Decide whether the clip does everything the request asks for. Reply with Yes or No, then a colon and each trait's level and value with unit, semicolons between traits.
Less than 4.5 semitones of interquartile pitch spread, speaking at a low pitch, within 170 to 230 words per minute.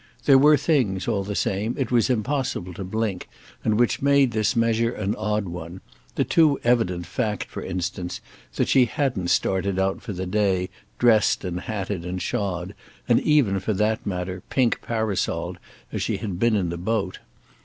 Yes: average, 4.1 semitones; low, 105 Hz; average, 175 wpm